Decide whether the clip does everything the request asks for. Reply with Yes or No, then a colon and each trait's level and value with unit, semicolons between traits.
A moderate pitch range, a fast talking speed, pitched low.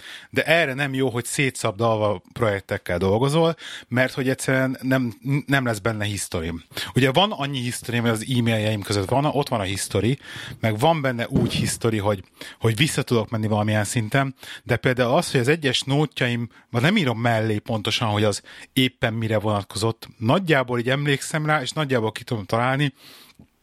Yes: average, 3.7 semitones; fast, 170 wpm; low, 120 Hz